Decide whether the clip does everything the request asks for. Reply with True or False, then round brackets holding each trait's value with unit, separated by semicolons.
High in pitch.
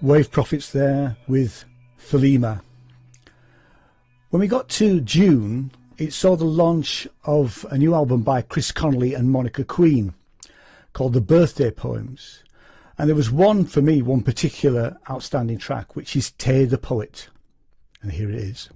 False (135 Hz)